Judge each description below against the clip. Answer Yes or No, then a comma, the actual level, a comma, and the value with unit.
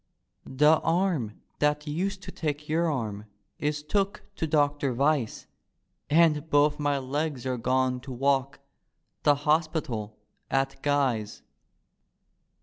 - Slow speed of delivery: Yes, slow, 125 wpm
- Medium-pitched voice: Yes, medium, 145 Hz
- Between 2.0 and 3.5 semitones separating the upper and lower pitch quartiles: Yes, average, 3.0 semitones